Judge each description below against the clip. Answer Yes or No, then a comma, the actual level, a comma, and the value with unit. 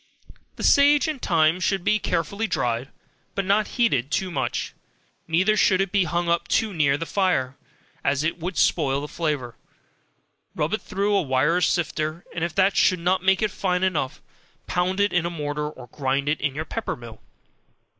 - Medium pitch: Yes, medium, 170 Hz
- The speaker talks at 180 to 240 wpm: Yes, average, 185 wpm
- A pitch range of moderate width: Yes, average, 4.7 semitones